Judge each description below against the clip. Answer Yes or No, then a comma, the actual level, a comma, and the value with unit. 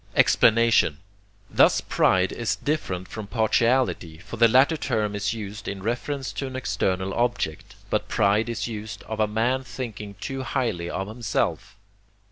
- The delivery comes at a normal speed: Yes, average, 150 wpm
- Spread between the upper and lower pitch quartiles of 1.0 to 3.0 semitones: No, average, 3.4 semitones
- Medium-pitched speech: No, low, 110 Hz